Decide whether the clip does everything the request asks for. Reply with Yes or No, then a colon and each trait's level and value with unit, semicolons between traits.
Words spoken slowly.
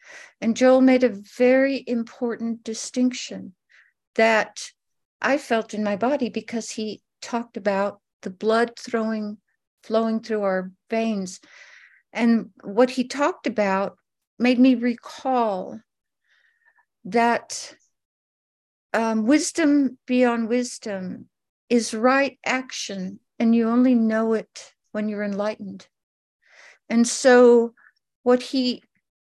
Yes: slow, 105 wpm